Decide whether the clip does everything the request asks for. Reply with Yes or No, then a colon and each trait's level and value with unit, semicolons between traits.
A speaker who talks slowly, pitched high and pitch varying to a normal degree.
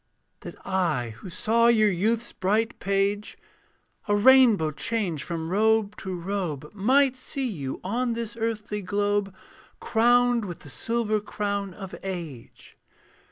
Yes: slow, 130 wpm; high, 205 Hz; average, 3.7 semitones